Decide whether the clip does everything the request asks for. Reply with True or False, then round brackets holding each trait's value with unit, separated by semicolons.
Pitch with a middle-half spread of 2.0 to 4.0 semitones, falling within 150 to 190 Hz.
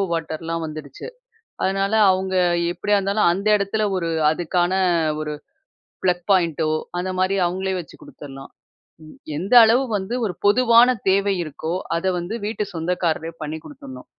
True (3.5 semitones; 185 Hz)